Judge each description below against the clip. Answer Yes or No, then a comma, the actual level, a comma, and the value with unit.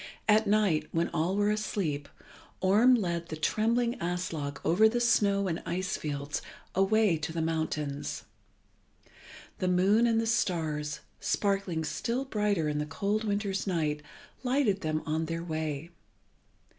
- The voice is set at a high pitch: No, medium, 180 Hz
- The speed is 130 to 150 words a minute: Yes, average, 140 wpm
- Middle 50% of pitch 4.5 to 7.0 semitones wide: Yes, average, 5.1 semitones